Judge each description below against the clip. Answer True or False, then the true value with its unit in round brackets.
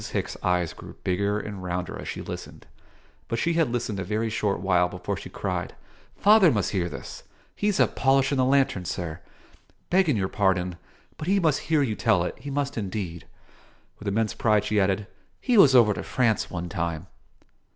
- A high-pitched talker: False (105 Hz)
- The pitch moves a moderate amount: False (6.9 semitones)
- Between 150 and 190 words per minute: True (185 wpm)